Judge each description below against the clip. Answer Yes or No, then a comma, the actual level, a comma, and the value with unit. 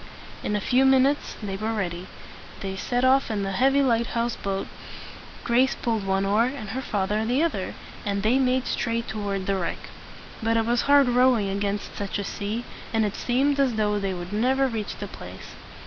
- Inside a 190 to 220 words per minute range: Yes, average, 195 wpm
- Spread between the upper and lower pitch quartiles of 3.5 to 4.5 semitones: Yes, average, 4.2 semitones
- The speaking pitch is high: Yes, high, 225 Hz